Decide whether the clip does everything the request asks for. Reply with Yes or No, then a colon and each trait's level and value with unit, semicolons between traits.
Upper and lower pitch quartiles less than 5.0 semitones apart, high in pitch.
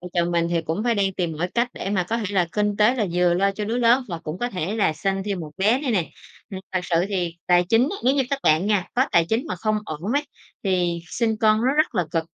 Yes: average, 4.4 semitones; high, 195 Hz